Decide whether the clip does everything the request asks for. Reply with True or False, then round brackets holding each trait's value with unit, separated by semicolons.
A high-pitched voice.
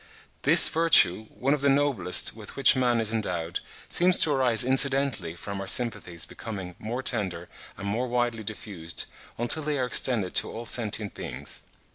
False (115 Hz)